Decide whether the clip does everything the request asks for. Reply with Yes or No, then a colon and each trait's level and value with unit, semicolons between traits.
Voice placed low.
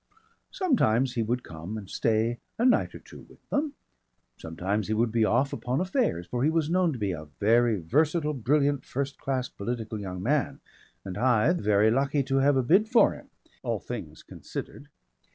Yes: low, 125 Hz